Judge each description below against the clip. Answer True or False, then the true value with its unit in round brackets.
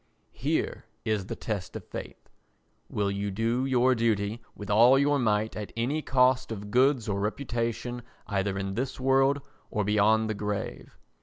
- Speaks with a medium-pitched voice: False (110 Hz)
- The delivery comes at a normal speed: True (155 wpm)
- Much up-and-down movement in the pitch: False (3.7 semitones)